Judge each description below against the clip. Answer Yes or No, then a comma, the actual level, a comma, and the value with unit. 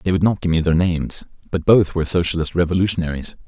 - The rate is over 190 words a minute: Yes, fast, 205 wpm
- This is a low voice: Yes, very low, 85 Hz